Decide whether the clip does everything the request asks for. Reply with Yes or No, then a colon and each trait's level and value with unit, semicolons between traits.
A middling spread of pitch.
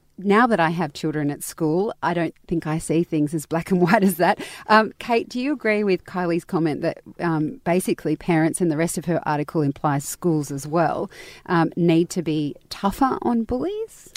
Yes: average, 3.9 semitones